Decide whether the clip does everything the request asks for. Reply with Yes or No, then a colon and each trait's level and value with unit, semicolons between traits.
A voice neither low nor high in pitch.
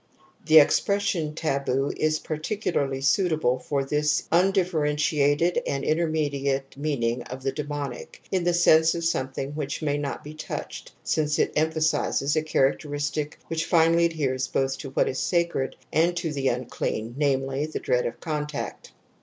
Yes: medium, 150 Hz